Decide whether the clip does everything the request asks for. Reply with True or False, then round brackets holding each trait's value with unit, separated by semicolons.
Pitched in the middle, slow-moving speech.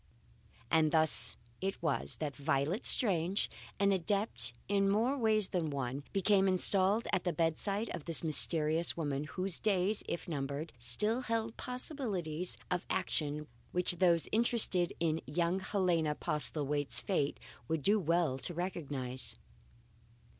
True (175 Hz; 130 wpm)